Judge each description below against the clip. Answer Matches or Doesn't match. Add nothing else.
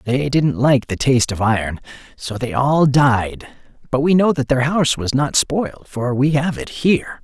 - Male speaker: Matches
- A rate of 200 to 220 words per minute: Matches